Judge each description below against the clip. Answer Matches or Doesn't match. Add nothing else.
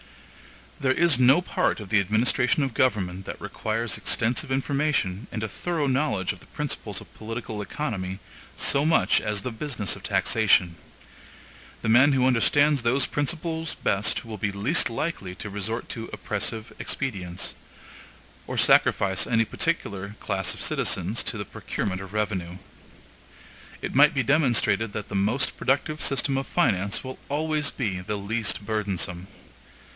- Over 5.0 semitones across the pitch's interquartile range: Matches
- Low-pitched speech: Matches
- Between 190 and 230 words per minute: Doesn't match